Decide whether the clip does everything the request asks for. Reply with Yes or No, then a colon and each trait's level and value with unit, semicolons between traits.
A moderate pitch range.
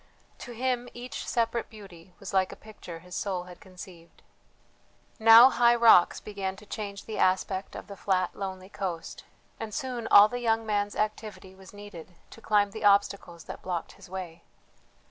Yes: average, 3.2 semitones